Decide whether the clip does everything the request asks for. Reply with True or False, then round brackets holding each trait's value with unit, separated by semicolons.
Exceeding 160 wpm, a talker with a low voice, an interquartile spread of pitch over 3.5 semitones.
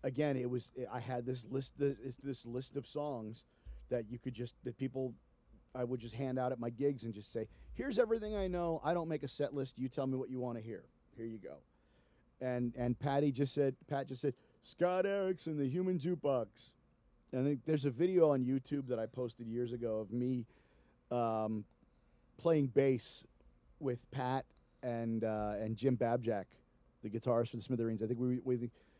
False (205 wpm; 130 Hz; 3.1 semitones)